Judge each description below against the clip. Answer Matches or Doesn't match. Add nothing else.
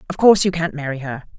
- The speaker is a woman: Matches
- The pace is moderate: Doesn't match